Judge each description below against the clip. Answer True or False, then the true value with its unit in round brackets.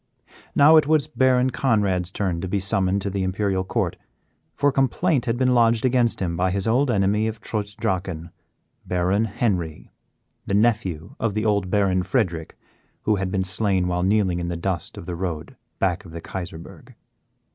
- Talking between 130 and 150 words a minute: False (180 wpm)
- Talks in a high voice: False (100 Hz)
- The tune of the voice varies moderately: True (3.8 semitones)